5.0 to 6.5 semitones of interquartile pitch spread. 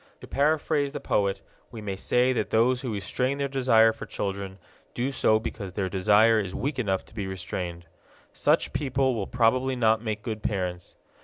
No: average, 4.5 semitones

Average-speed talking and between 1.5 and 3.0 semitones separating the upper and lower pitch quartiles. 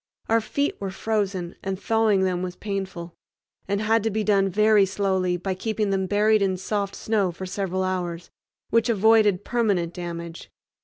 Yes: average, 165 wpm; average, 2.7 semitones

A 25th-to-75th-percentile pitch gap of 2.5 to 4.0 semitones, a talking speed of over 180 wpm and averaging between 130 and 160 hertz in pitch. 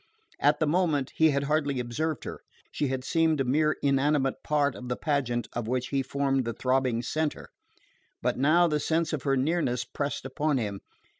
Yes: average, 3.1 semitones; average, 190 wpm; medium, 140 Hz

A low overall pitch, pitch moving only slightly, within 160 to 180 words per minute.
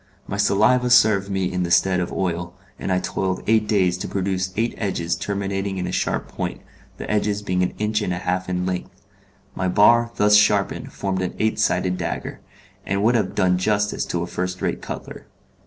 No: very low, 95 Hz; narrow, 2.3 semitones; average, 200 wpm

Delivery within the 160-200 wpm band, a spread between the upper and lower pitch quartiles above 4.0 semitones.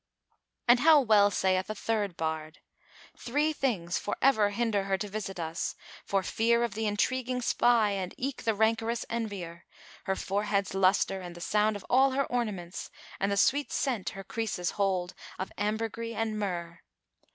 No: average, 170 wpm; average, 3.5 semitones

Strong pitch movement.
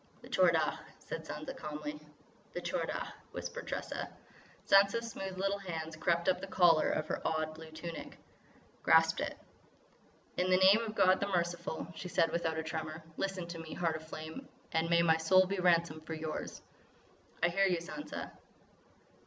No: average, 2.9 semitones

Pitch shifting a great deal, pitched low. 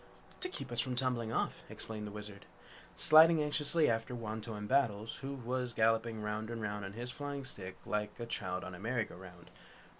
No: average, 3.5 semitones; low, 115 Hz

